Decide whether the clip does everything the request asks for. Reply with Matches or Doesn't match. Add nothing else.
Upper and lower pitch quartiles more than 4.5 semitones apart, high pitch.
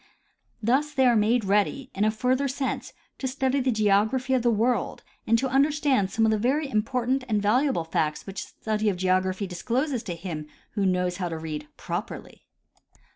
Matches